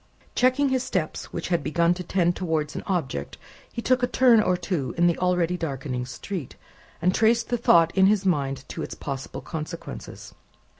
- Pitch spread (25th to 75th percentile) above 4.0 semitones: Yes, wide, 5.4 semitones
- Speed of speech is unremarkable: Yes, average, 185 wpm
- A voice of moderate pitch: Yes, medium, 175 Hz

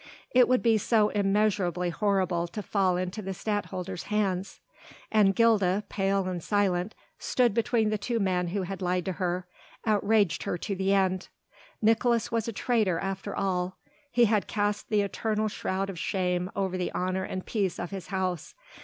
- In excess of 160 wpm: Yes, average, 170 wpm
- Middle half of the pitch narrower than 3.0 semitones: Yes, narrow, 2.6 semitones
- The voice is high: Yes, high, 195 Hz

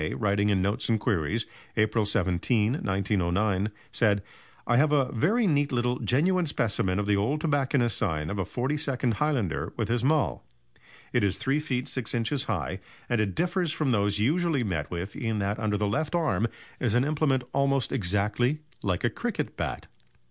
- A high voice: No, low, 115 Hz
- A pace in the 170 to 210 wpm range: Yes, average, 175 wpm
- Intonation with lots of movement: Yes, wide, 5.7 semitones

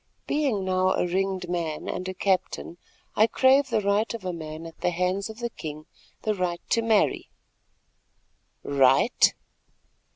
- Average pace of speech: Yes, average, 150 wpm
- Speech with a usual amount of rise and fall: Yes, average, 4.1 semitones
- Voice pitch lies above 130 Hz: Yes, medium, 185 Hz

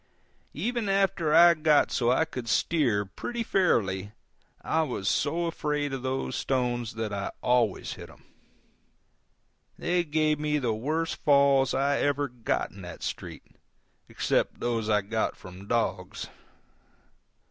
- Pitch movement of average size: No, wide, 5.7 semitones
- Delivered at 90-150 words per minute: Yes, average, 140 wpm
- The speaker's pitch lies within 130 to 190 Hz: Yes, low, 135 Hz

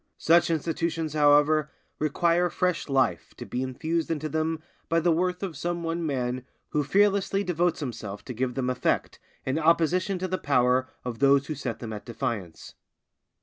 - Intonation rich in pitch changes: No, average, 4.6 semitones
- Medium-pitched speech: Yes, medium, 155 Hz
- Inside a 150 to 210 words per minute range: Yes, average, 170 wpm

